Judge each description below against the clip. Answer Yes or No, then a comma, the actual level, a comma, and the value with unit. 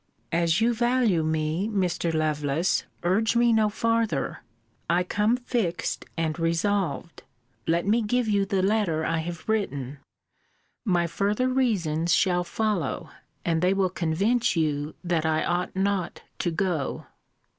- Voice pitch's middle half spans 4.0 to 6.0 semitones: Yes, average, 4.6 semitones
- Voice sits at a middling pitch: Yes, medium, 180 Hz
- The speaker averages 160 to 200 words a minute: No, slow, 135 wpm